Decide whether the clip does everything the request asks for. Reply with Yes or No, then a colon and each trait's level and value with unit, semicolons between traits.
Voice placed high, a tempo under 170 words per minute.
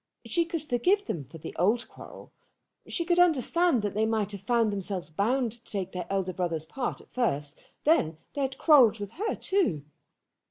No: high, 220 Hz; average, 190 wpm